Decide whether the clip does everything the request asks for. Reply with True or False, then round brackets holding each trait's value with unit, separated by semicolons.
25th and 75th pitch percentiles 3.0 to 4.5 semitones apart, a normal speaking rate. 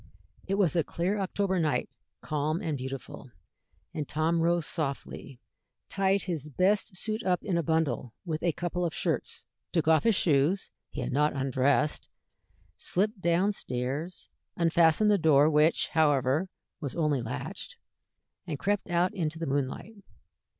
True (4.1 semitones; 150 wpm)